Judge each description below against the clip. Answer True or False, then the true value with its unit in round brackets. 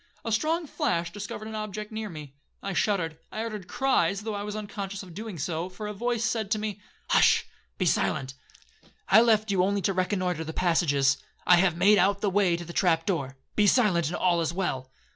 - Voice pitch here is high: True (195 Hz)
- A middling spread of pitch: True (3.8 semitones)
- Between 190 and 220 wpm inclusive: True (200 wpm)